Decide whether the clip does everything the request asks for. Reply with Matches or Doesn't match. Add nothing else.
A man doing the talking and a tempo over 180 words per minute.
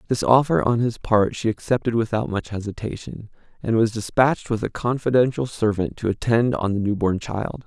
Matches